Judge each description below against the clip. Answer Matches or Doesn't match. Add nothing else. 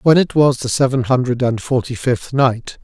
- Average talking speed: Doesn't match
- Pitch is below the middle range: Matches